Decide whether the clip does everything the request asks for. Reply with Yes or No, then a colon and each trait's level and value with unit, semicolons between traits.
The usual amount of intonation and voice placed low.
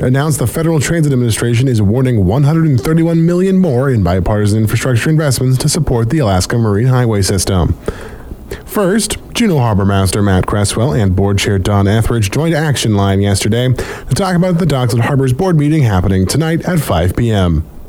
No: wide, 7.2 semitones; low, 120 Hz